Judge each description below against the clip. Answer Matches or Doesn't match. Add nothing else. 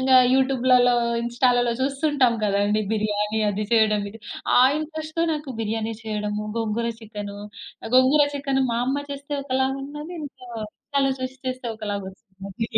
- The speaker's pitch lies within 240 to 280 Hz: Matches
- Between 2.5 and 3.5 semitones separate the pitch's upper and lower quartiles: Doesn't match